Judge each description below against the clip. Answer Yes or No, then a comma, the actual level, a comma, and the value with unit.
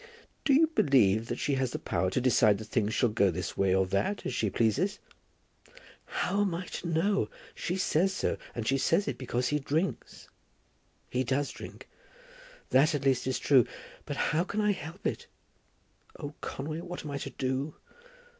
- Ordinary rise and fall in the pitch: No, wide, 6.4 semitones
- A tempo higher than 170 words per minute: Yes, average, 190 wpm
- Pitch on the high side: No, low, 135 Hz